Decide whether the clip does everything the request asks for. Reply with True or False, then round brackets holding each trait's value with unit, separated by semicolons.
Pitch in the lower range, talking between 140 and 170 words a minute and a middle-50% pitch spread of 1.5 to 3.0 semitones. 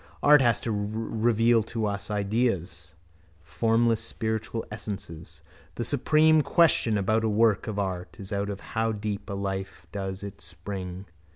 True (105 Hz; 150 wpm; 2.7 semitones)